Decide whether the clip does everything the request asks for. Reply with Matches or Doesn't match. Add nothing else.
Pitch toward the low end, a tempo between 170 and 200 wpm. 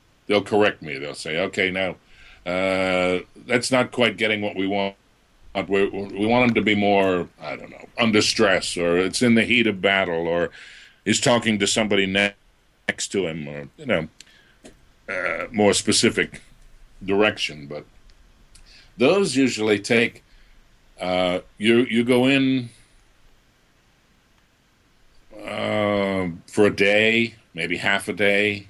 Doesn't match